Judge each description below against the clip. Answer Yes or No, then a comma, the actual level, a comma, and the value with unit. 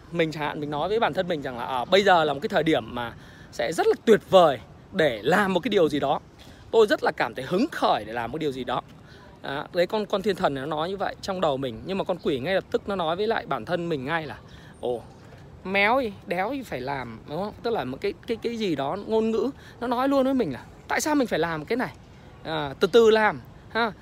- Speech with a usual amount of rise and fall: No, wide, 7.7 semitones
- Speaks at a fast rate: Yes, fast, 285 wpm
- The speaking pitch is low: No, high, 190 Hz